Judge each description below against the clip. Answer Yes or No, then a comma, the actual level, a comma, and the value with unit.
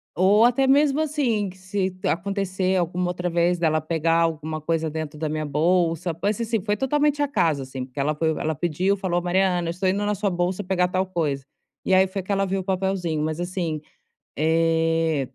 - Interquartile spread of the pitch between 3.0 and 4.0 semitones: Yes, average, 3.3 semitones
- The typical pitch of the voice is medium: Yes, medium, 180 Hz